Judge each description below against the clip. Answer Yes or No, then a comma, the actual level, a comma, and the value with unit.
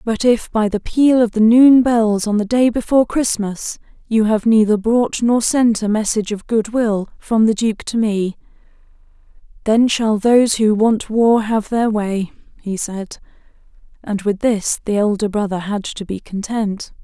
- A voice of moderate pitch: No, high, 220 Hz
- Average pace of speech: Yes, average, 180 wpm